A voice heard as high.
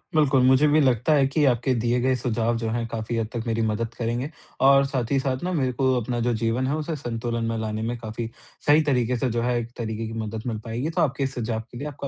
No: low, 120 Hz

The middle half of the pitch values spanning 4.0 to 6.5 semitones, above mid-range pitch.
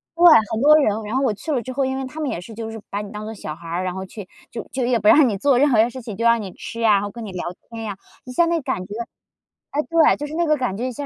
Yes: average, 4.6 semitones; high, 230 Hz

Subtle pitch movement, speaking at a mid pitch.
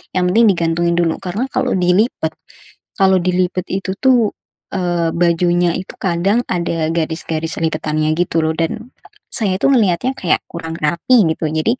No: average, 3.0 semitones; medium, 175 Hz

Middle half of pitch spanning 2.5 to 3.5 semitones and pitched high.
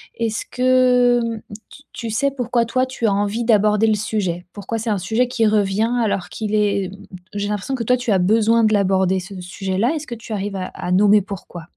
Yes: average, 3.0 semitones; high, 215 Hz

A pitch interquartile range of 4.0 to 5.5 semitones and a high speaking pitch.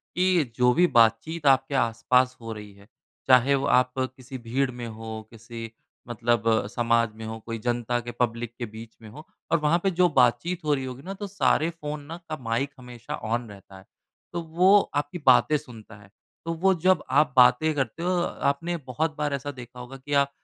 No: average, 4.7 semitones; low, 130 Hz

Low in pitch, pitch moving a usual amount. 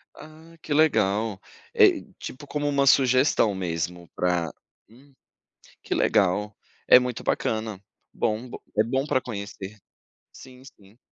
No: low, 115 Hz; wide, 5.7 semitones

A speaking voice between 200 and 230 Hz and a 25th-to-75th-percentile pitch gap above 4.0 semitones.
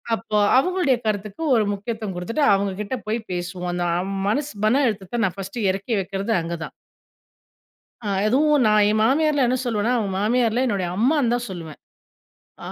Yes: high, 215 Hz; average, 4.5 semitones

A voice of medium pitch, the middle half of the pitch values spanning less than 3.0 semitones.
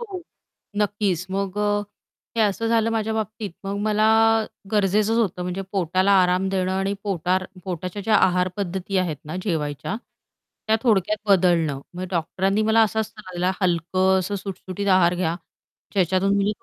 No: high, 195 Hz; narrow, 2.4 semitones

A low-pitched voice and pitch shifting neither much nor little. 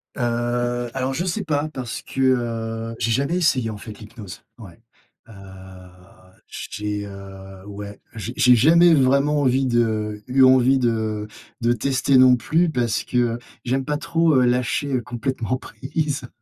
Yes: low, 125 Hz; average, 3.1 semitones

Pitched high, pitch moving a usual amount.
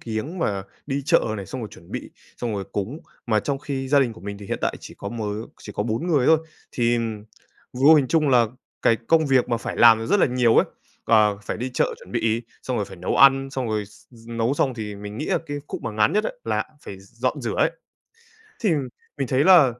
No: low, 120 Hz; average, 4.3 semitones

